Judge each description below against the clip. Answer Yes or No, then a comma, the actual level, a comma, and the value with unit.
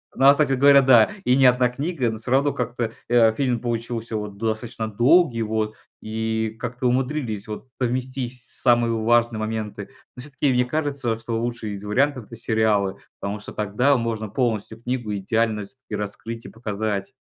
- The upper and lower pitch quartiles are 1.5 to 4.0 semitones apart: Yes, narrow, 2.5 semitones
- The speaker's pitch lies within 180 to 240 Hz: No, low, 115 Hz